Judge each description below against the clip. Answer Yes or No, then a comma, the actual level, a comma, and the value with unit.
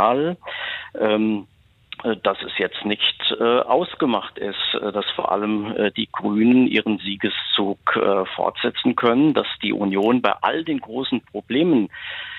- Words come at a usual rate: No, slow, 110 wpm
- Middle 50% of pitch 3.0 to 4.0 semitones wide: Yes, average, 3.4 semitones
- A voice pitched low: Yes, low, 110 Hz